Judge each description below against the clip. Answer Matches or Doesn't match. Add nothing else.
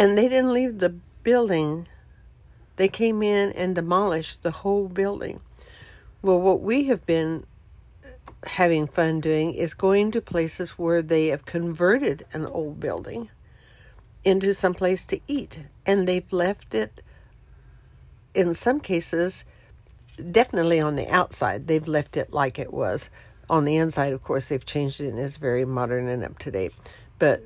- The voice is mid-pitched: Matches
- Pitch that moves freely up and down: Doesn't match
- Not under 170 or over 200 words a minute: Doesn't match